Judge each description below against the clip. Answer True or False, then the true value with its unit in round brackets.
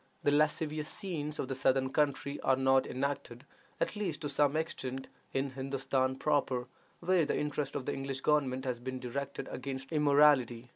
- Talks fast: False (175 wpm)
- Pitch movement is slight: True (2.2 semitones)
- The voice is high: False (140 Hz)